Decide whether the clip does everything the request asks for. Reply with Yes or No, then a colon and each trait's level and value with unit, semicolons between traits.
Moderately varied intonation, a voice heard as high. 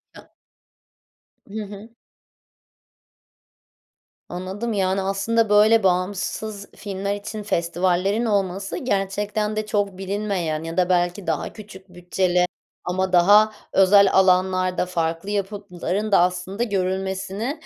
No: narrow, 2.2 semitones; high, 195 Hz